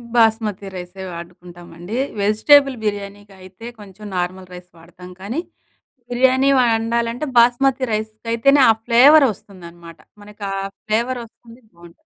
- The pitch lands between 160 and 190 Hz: No, high, 215 Hz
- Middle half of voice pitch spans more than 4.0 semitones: Yes, average, 4.7 semitones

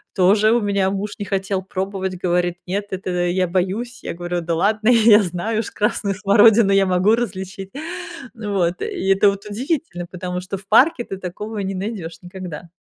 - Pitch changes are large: No, narrow, 2.5 semitones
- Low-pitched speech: No, high, 195 Hz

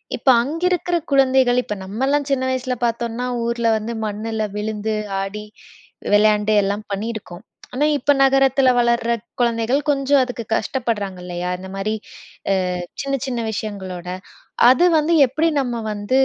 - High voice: Yes, high, 235 Hz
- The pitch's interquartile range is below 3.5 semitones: No, average, 4.0 semitones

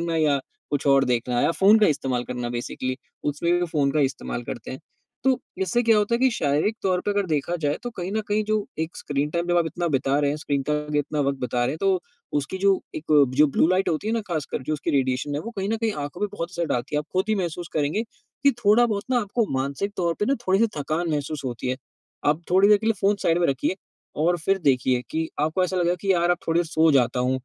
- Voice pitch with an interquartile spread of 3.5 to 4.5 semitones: No, wide, 5.5 semitones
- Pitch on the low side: No, medium, 160 Hz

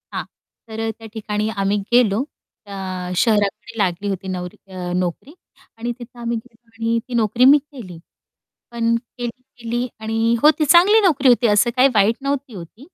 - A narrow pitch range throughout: No, average, 3.6 semitones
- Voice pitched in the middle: No, high, 230 Hz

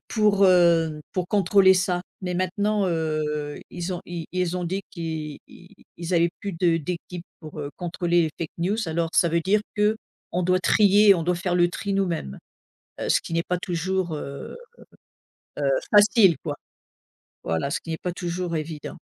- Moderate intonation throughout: No, narrow, 2.3 semitones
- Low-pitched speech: No, medium, 175 Hz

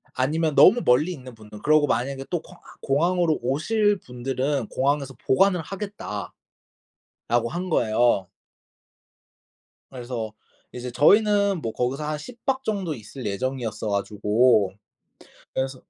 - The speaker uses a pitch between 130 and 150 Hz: Yes, low, 135 Hz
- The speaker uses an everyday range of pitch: No, wide, 6.4 semitones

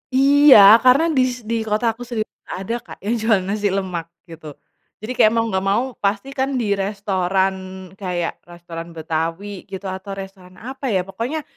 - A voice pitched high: Yes, high, 200 Hz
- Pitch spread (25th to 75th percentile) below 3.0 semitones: No, average, 4.1 semitones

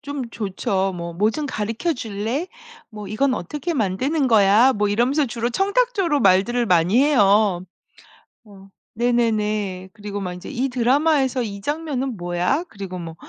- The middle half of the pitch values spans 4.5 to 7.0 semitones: Yes, wide, 5.5 semitones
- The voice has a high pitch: Yes, high, 225 Hz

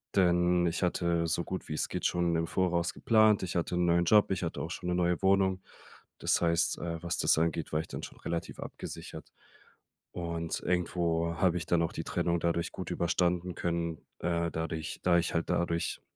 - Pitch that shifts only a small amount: Yes, narrow, 1.1 semitones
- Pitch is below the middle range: Yes, very low, 85 Hz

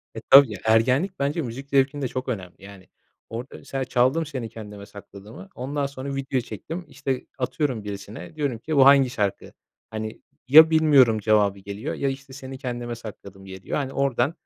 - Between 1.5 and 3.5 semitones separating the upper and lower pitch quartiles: No, average, 4.3 semitones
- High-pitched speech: No, low, 130 Hz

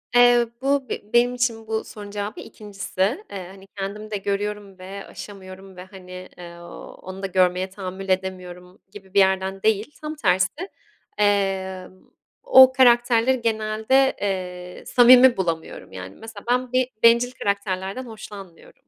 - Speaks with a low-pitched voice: No, high, 200 Hz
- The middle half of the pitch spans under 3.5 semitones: No, average, 3.9 semitones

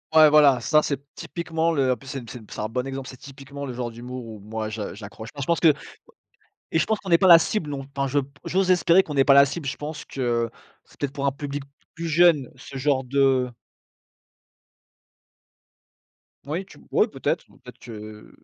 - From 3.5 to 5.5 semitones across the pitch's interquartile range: Yes, average, 3.8 semitones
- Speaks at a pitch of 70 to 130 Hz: No, medium, 140 Hz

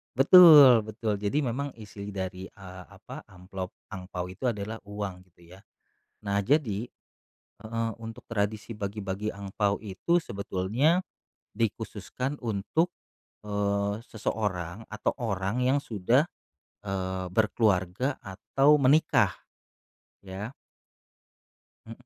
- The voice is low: Yes, low, 105 Hz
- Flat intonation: No, average, 3.5 semitones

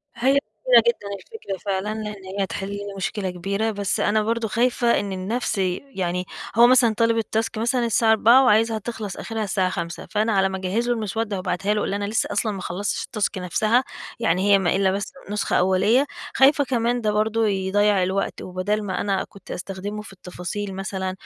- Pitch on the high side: Yes, high, 205 Hz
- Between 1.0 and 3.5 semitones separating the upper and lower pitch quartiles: Yes, average, 2.8 semitones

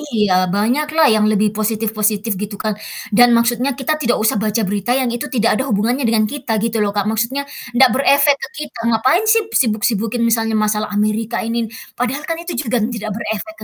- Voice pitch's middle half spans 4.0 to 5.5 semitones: No, average, 3.3 semitones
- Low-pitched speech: No, high, 230 Hz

